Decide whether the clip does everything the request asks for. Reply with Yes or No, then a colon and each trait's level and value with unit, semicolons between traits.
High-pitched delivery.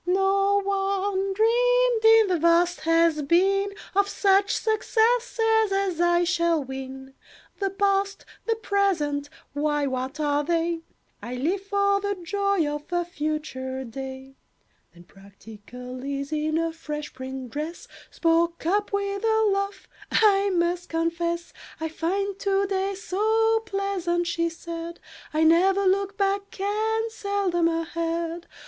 Yes: very high, 350 Hz